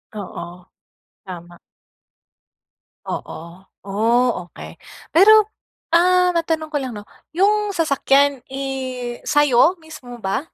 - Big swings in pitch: Yes, wide, 6.3 semitones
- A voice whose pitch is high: Yes, very high, 270 Hz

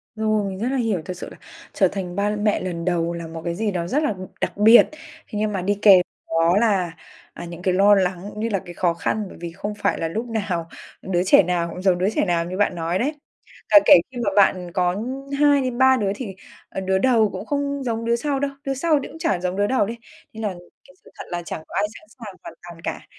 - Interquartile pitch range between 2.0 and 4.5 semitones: Yes, average, 4.1 semitones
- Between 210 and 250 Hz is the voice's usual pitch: No, high, 200 Hz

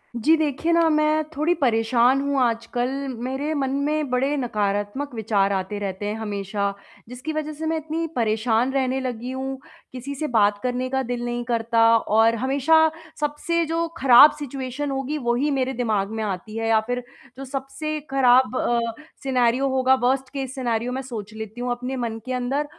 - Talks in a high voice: Yes, very high, 255 Hz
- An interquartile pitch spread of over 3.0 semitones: Yes, average, 3.6 semitones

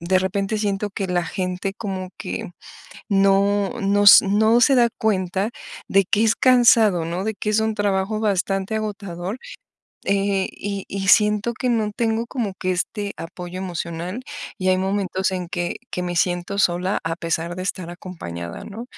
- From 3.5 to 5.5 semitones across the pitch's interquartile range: No, narrow, 2.6 semitones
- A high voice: Yes, high, 195 Hz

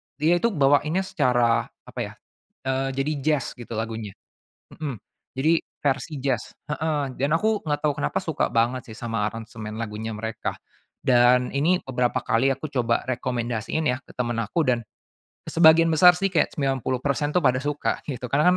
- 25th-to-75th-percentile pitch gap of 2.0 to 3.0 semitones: No, average, 4.2 semitones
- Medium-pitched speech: No, low, 130 Hz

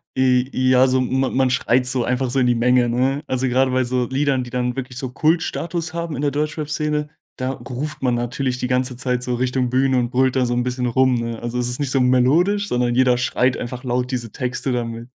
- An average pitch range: No, narrow, 1.3 semitones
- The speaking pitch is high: No, low, 125 Hz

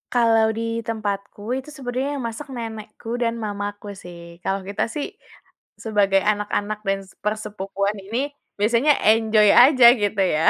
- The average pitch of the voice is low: No, high, 215 Hz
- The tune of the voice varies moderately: No, narrow, 2.2 semitones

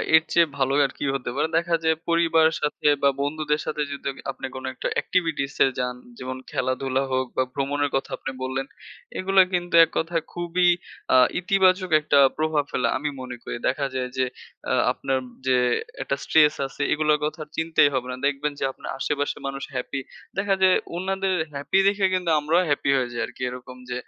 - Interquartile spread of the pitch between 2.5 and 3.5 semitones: No, average, 3.9 semitones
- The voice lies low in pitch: No, medium, 150 Hz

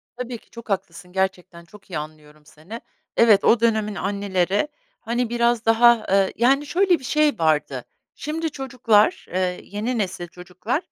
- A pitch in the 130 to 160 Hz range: No, high, 210 Hz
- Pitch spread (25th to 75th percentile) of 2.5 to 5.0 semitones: Yes, average, 4.7 semitones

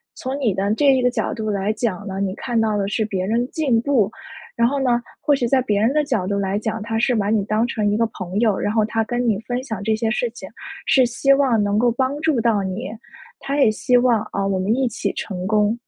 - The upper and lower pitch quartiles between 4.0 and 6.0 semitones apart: No, average, 3.3 semitones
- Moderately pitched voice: No, high, 225 Hz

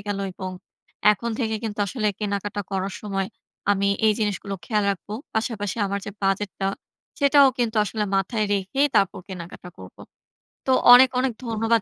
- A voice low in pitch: No, high, 205 Hz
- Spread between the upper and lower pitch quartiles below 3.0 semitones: Yes, narrow, 2.5 semitones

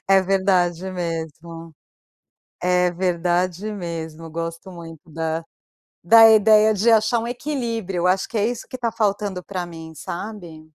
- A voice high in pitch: No, medium, 180 Hz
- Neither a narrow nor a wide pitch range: Yes, average, 4.2 semitones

